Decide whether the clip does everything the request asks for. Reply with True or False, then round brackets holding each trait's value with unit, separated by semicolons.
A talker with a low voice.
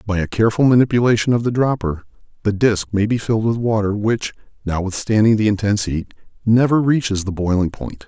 True (110 Hz)